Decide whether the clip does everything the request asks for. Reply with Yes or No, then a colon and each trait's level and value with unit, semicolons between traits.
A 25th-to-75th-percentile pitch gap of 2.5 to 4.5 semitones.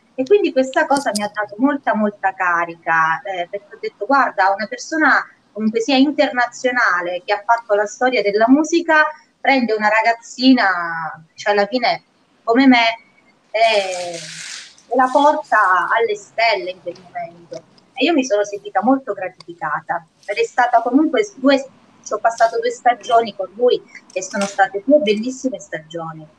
No: average, 5.3 semitones